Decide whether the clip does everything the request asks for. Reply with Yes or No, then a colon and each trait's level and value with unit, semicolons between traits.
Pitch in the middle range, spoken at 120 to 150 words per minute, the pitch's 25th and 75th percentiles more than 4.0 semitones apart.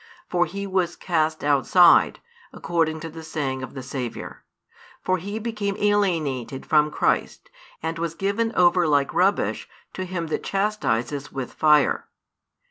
Yes: medium, 165 Hz; average, 140 wpm; average, 4.4 semitones